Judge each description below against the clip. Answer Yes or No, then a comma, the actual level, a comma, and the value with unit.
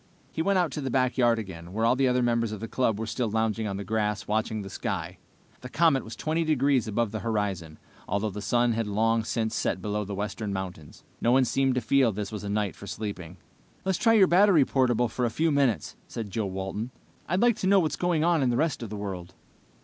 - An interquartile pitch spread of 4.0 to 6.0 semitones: Yes, average, 4.5 semitones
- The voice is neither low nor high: No, low, 115 Hz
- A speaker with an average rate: No, fast, 240 wpm